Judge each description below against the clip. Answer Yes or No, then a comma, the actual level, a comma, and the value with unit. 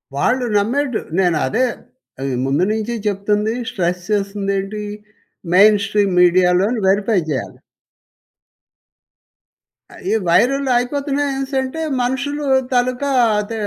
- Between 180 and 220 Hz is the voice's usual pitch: Yes, high, 215 Hz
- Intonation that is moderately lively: Yes, average, 4.9 semitones